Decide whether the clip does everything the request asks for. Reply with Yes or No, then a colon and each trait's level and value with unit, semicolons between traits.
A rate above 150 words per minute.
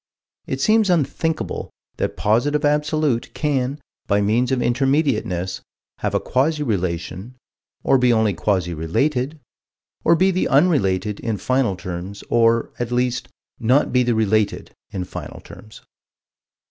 No: slow, 135 wpm